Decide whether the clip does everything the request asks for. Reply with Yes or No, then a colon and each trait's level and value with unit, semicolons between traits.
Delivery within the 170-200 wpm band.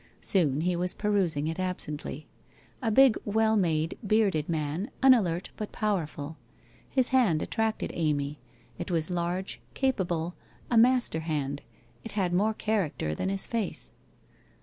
No: slow, 135 wpm